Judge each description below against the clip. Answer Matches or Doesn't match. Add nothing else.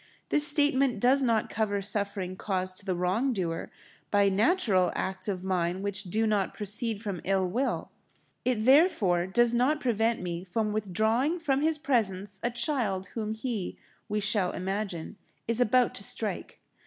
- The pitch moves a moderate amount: Matches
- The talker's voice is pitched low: Doesn't match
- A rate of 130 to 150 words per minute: Doesn't match